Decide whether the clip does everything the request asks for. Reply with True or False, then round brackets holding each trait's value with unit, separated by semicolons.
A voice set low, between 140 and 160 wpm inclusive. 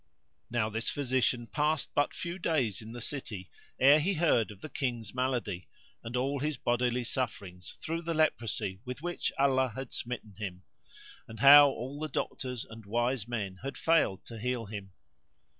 False (125 Hz; 170 wpm)